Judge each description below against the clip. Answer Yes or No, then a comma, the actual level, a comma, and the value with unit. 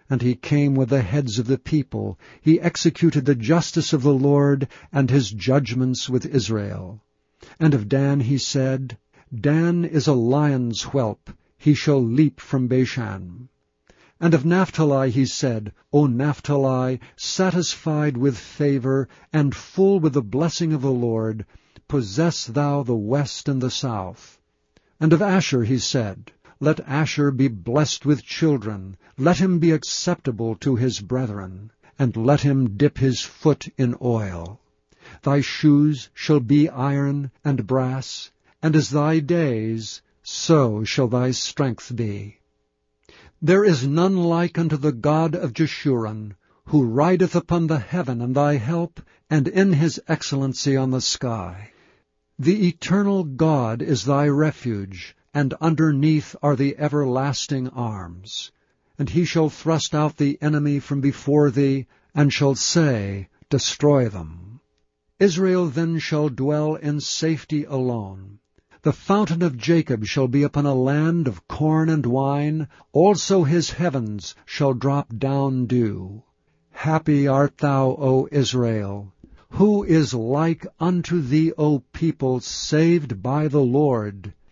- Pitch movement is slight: No, average, 3.9 semitones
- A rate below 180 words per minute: Yes, average, 140 wpm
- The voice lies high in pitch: No, medium, 140 Hz